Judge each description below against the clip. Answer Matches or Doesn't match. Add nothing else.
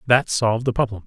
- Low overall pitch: Matches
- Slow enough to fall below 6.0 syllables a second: Doesn't match